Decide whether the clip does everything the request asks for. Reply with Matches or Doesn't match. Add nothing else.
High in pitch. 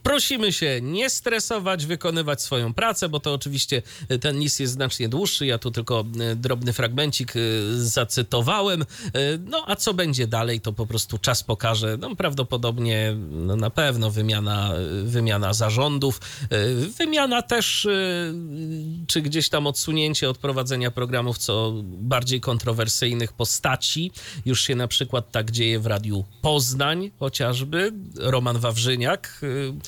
Doesn't match